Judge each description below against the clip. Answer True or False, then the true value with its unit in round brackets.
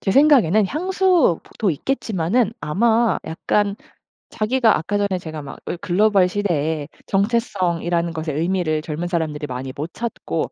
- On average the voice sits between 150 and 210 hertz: True (185 Hz)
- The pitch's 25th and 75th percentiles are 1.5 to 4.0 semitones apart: False (5.5 semitones)